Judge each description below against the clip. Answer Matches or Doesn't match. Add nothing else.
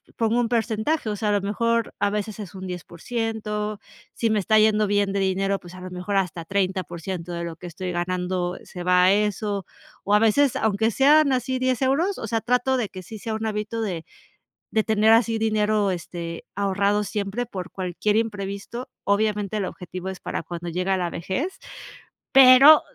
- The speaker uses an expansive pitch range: Doesn't match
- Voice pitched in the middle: Doesn't match